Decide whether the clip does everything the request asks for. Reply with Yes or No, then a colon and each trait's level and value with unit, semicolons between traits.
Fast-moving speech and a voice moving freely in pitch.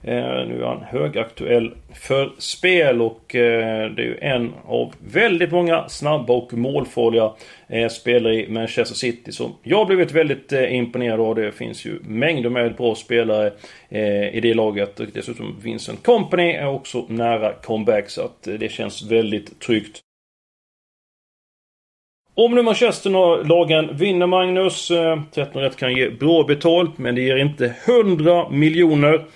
No: average, 140 wpm; wide, 6.6 semitones